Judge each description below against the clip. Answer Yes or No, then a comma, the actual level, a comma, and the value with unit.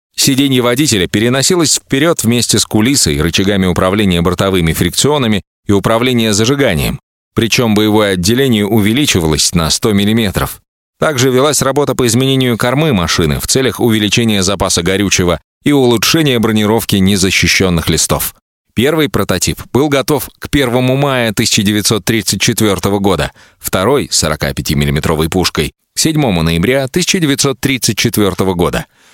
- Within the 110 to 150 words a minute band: Yes, average, 115 wpm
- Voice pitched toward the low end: Yes, low, 110 Hz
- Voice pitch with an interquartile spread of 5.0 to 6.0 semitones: Yes, wide, 5.5 semitones